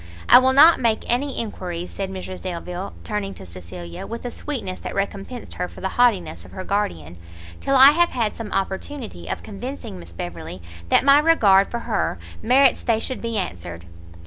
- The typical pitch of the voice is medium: No, high, 200 Hz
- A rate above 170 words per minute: Yes, average, 185 wpm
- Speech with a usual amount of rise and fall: No, wide, 5.9 semitones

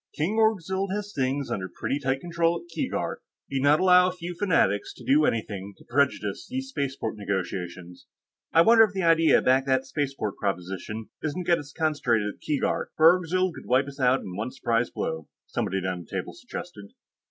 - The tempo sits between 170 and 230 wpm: Yes, average, 200 wpm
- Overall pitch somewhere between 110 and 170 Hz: Yes, medium, 140 Hz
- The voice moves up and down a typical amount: No, wide, 8.2 semitones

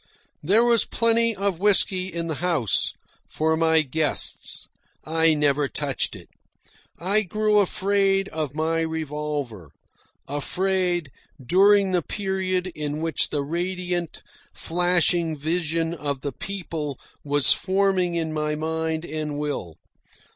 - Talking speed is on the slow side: Yes, slow, 120 wpm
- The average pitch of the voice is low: No, medium, 165 Hz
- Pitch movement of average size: Yes, average, 3.7 semitones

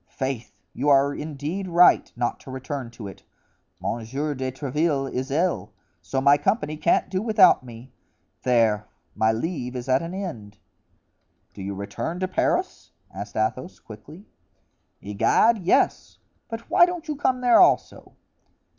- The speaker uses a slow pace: No, average, 145 wpm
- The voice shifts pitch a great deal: Yes, wide, 7.1 semitones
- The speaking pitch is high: No, medium, 140 Hz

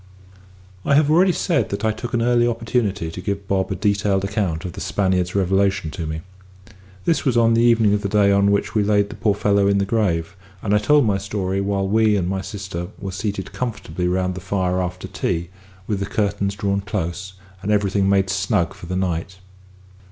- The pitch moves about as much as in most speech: No, narrow, 2.1 semitones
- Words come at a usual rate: No, fast, 210 wpm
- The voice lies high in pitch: No, low, 100 Hz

